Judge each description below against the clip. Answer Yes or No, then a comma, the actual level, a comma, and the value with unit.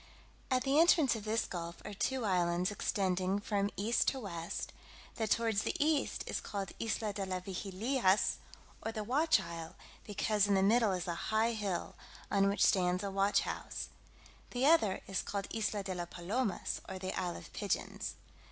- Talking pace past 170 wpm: Yes, average, 180 wpm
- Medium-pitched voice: No, high, 200 Hz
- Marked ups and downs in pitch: No, average, 3.3 semitones